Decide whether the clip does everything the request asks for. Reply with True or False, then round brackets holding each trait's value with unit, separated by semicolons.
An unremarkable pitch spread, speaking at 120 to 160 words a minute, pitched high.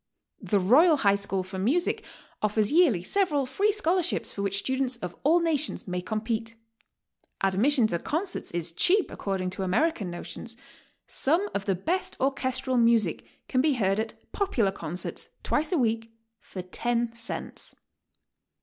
False (7.4 semitones; 150 wpm; 235 Hz)